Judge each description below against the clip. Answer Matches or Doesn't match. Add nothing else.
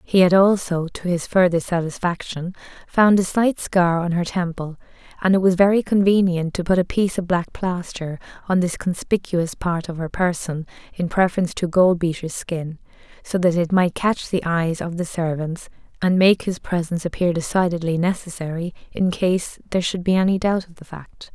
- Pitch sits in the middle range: Matches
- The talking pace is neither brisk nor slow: Matches